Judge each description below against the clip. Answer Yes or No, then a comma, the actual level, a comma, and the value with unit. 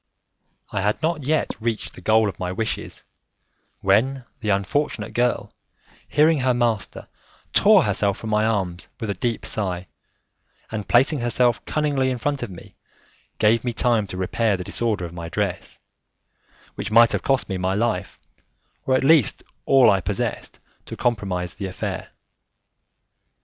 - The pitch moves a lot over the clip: No, average, 4.1 semitones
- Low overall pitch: Yes, low, 110 Hz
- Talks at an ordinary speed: Yes, average, 155 wpm